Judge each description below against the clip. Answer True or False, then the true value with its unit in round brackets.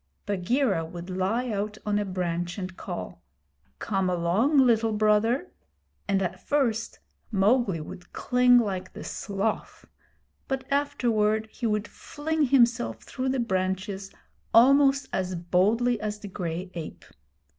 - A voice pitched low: False (210 Hz)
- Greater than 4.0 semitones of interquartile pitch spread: True (4.7 semitones)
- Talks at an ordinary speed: False (130 wpm)